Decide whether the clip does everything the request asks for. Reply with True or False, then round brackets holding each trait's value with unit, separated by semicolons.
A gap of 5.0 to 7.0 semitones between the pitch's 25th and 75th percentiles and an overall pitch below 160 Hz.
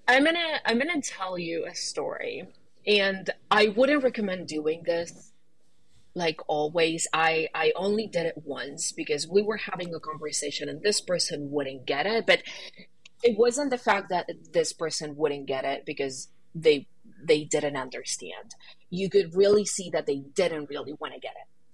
False (5.6 semitones; 175 Hz)